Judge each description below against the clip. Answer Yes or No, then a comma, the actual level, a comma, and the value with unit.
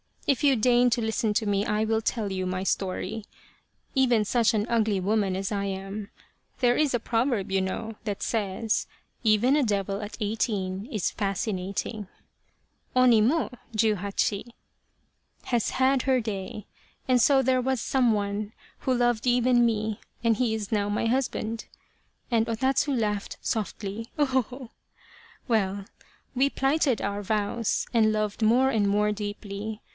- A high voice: Yes, high, 220 Hz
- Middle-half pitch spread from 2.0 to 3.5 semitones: Yes, average, 3.1 semitones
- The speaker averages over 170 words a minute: No, average, 160 wpm